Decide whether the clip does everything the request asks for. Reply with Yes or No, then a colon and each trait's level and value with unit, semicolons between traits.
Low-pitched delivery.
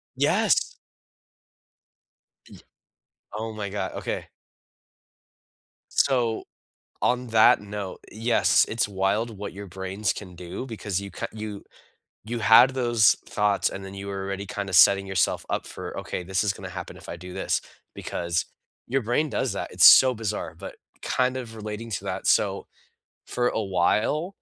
Yes: low, 105 Hz